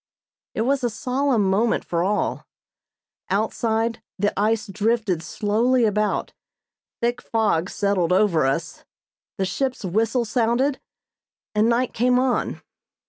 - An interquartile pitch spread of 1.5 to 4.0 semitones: Yes, average, 3.2 semitones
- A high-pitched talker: Yes, high, 220 Hz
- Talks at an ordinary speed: No, slow, 120 wpm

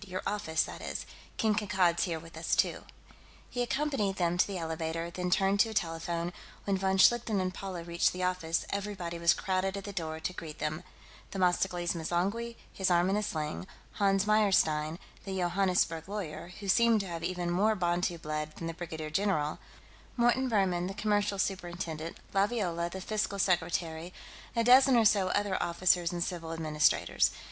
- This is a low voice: No, medium, 180 Hz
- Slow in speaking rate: No, average, 175 wpm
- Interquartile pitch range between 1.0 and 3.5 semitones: Yes, average, 3.0 semitones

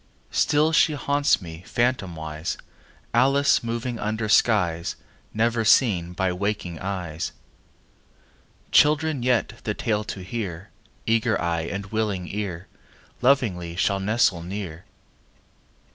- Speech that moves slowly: Yes, slow, 110 wpm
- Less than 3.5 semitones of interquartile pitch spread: No, average, 5.0 semitones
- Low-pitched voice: Yes, low, 105 Hz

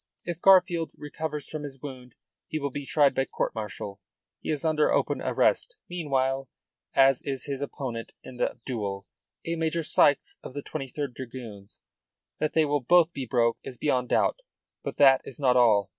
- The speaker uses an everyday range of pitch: Yes, average, 3.6 semitones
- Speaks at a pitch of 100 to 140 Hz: Yes, low, 135 Hz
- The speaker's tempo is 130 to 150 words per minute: No, average, 175 wpm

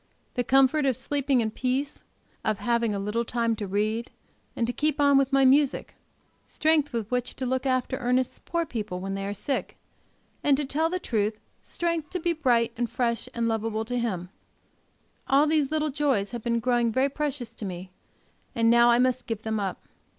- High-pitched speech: Yes, high, 245 Hz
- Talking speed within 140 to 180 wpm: No, average, 195 wpm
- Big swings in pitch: No, average, 3.7 semitones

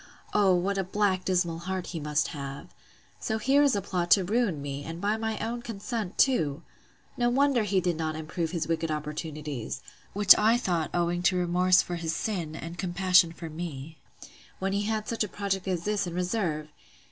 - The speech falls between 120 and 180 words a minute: No, average, 190 wpm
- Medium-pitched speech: Yes, medium, 180 Hz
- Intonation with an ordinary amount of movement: Yes, average, 4.0 semitones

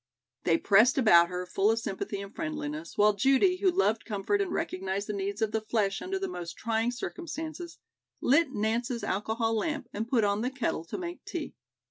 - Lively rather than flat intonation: Yes, wide, 6.2 semitones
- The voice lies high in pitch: Yes, high, 225 Hz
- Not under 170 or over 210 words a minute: Yes, average, 190 wpm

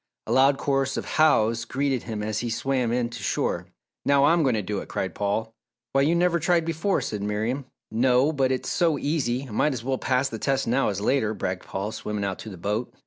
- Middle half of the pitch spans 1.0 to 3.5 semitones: No, average, 4.4 semitones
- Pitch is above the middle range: No, low, 125 Hz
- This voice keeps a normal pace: No, fast, 230 wpm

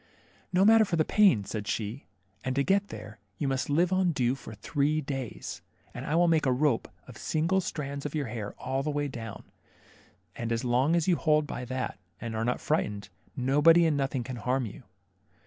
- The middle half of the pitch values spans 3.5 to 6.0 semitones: Yes, average, 4.7 semitones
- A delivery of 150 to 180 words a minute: No, fast, 205 wpm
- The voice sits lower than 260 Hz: Yes, medium, 140 Hz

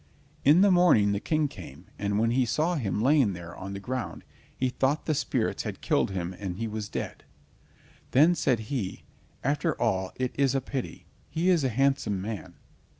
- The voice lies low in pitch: Yes, low, 120 Hz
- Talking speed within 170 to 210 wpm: Yes, average, 185 wpm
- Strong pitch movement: Yes, wide, 6.2 semitones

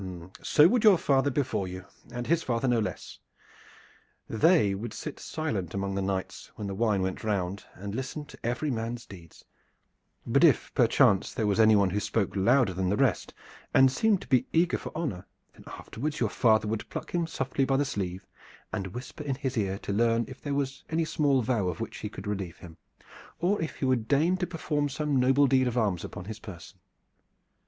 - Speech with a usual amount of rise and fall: No, wide, 6.1 semitones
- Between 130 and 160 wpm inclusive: No, average, 200 wpm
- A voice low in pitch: Yes, low, 115 Hz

